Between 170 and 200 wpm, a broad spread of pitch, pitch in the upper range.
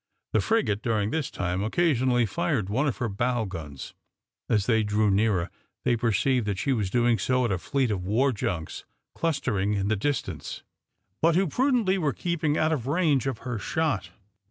No: average, 180 wpm; wide, 5.9 semitones; low, 120 Hz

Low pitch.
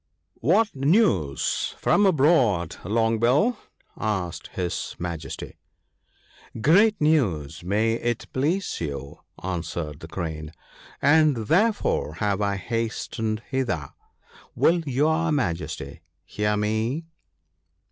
Yes: low, 110 Hz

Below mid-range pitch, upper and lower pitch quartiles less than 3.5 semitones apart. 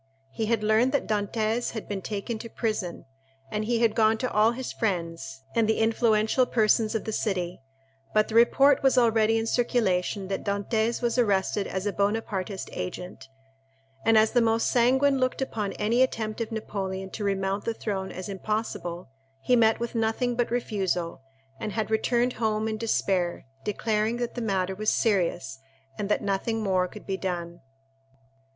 No: high, 215 Hz; average, 3.0 semitones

